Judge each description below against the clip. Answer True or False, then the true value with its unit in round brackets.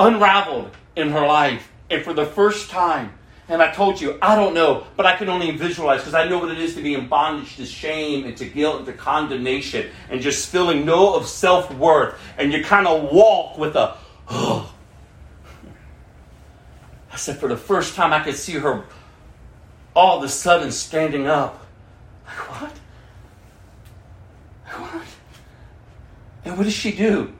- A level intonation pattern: False (4.8 semitones)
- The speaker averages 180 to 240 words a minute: False (170 wpm)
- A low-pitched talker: False (155 Hz)